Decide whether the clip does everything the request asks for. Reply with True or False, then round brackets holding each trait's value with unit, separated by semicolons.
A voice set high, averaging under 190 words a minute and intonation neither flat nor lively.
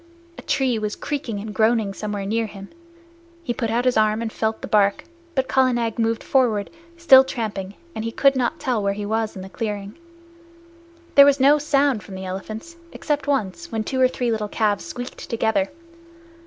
False (225 Hz; 195 wpm; 4.0 semitones)